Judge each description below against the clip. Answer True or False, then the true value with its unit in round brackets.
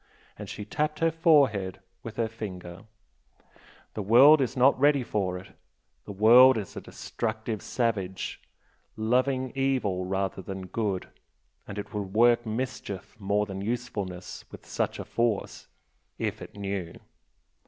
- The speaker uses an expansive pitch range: False (4.5 semitones)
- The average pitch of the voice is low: True (110 Hz)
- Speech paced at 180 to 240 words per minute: False (140 wpm)